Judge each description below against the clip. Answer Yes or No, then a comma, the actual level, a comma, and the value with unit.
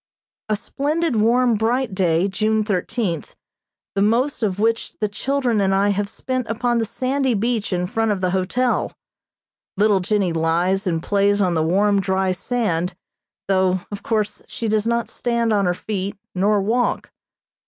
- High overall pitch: Yes, high, 210 Hz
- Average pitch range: Yes, average, 3.6 semitones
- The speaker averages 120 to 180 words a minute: Yes, average, 165 wpm